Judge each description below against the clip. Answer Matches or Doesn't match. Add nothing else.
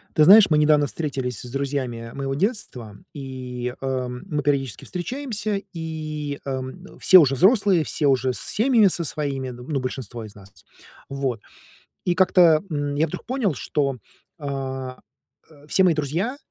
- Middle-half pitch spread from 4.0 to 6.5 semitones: Matches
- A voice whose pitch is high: Doesn't match